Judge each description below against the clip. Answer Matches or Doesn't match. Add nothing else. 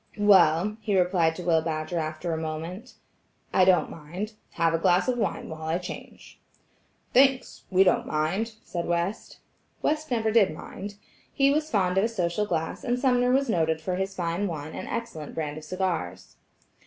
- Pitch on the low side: Doesn't match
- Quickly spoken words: Doesn't match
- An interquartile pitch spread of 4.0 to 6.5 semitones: Matches